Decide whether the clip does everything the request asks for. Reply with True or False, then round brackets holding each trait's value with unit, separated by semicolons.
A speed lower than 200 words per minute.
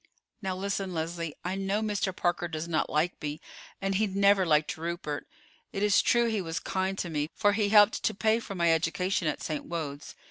False (205 wpm)